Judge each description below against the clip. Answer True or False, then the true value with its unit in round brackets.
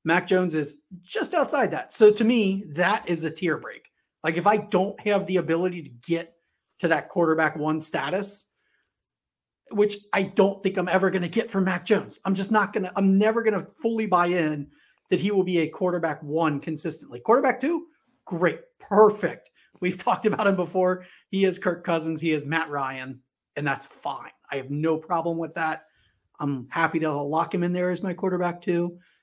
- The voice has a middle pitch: True (180 Hz)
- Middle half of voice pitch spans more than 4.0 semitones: False (3.7 semitones)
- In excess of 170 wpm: True (195 wpm)